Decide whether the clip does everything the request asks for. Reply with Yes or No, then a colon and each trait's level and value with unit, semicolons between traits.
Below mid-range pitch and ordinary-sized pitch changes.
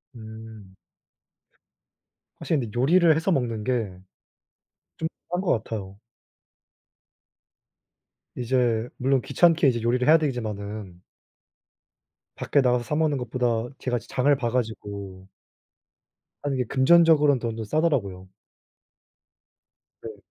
Yes: low, 125 Hz; average, 4.6 semitones